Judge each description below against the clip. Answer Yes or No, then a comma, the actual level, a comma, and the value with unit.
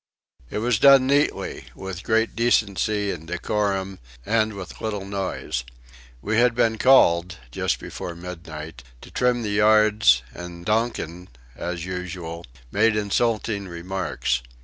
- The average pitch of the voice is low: Yes, low, 100 Hz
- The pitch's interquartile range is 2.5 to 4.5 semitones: Yes, average, 4.0 semitones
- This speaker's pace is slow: Yes, slow, 125 wpm